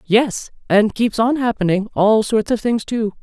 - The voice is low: No, high, 220 Hz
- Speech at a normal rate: Yes, average, 185 wpm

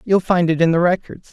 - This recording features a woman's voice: No, male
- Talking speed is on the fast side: Yes, fast, 275 wpm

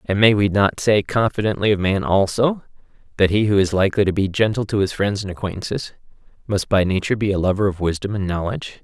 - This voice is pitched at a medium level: No, low, 100 Hz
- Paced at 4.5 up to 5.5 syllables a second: No, 6.3 syllables/s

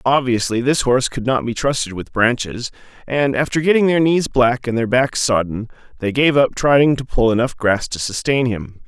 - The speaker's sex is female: No, male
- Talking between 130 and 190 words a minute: No, fast, 205 wpm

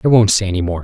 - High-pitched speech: No, low, 100 Hz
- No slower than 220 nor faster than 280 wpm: No, fast, 360 wpm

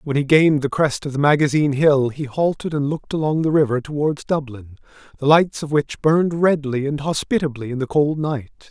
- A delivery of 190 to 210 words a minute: Yes, fast, 205 wpm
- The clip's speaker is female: No, male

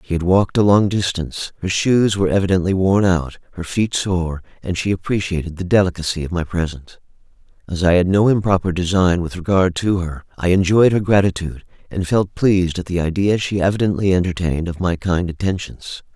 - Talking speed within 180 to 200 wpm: Yes, average, 185 wpm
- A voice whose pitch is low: Yes, very low, 90 Hz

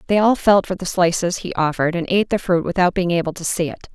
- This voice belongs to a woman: Yes, female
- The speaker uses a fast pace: Yes, fast, 275 wpm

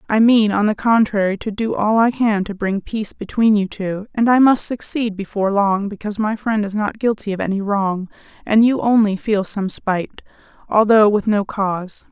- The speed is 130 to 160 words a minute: No, fast, 205 wpm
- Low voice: No, high, 210 Hz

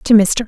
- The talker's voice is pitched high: Yes, high, 215 Hz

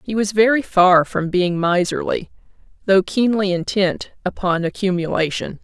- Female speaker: Yes, female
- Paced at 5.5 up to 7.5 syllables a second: No, 4.6 syllables/s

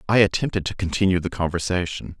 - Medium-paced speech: Yes, average, 165 wpm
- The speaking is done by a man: Yes, male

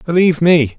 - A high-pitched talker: No, medium, 160 Hz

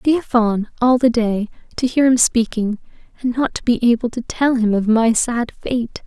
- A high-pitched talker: Yes, high, 235 Hz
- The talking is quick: Yes, fast, 230 wpm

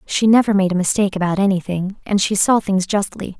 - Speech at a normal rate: No, fast, 210 wpm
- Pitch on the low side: No, high, 195 Hz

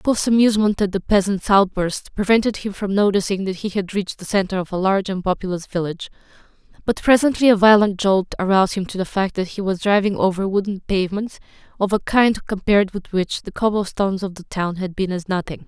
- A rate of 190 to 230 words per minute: Yes, fast, 205 wpm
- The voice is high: Yes, high, 195 Hz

